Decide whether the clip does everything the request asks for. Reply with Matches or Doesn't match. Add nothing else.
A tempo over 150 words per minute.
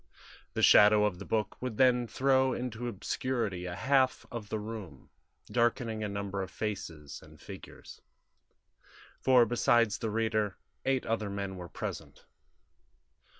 Doesn't match